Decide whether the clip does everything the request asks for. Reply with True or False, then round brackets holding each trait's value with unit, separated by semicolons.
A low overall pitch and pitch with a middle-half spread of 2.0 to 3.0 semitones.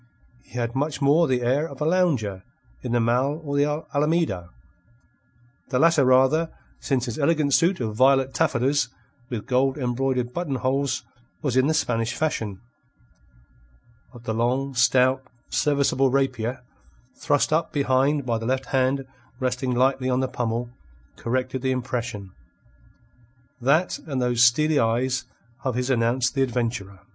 True (130 Hz; 2.6 semitones)